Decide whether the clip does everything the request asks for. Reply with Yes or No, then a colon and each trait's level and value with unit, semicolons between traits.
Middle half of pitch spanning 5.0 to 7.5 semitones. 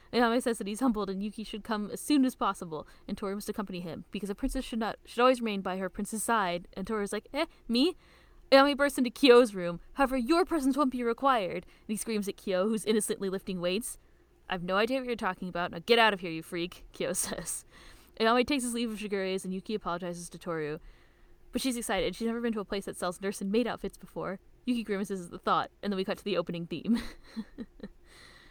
No: average, 4.1 semitones